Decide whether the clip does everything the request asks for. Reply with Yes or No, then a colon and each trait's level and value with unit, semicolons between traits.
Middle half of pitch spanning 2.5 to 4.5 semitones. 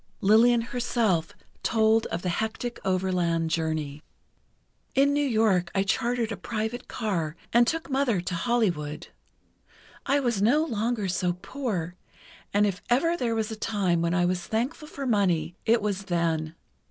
No: average, 5.3 semitones